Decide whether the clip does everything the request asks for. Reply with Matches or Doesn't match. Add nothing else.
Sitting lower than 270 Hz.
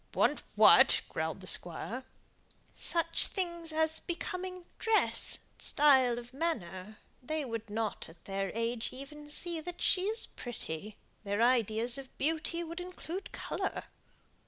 Doesn't match